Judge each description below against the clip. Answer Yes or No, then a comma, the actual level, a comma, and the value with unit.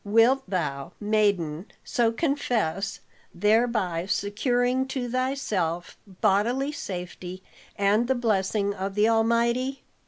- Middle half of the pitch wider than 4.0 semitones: Yes, average, 4.4 semitones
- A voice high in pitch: Yes, high, 215 Hz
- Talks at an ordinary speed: No, slow, 100 wpm